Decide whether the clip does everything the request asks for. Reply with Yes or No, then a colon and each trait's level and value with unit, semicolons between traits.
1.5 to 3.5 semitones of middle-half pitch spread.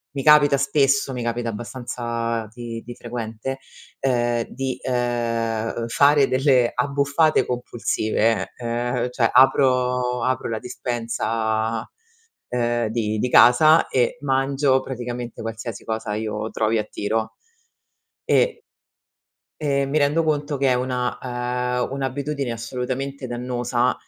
Yes: narrow, 2.5 semitones